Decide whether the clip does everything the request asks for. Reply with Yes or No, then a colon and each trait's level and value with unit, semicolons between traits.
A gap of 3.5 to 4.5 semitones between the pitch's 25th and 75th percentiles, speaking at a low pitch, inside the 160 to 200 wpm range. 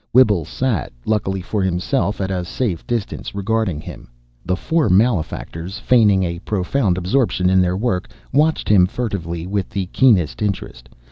No: average, 3.8 semitones; very low, 95 Hz; average, 150 wpm